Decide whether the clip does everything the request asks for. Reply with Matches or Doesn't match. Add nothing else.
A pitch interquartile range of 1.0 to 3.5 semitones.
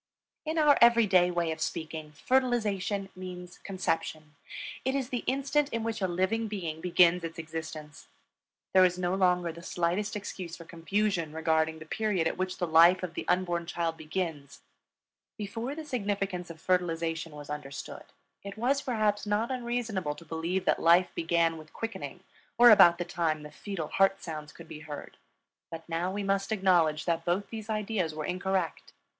Doesn't match